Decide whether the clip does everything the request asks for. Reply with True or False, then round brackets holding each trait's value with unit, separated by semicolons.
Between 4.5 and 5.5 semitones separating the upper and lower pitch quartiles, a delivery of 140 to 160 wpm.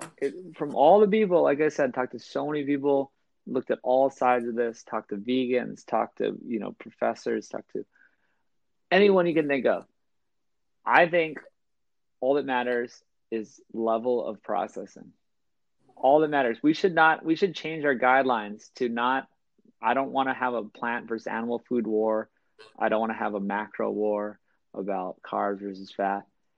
False (4.9 semitones; 180 wpm)